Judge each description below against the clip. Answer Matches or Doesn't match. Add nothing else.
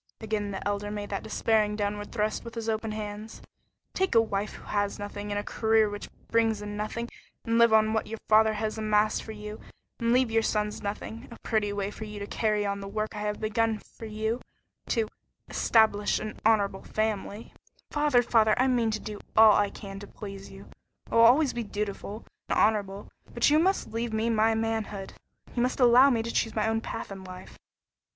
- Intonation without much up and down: Matches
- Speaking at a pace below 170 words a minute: Doesn't match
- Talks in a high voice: Matches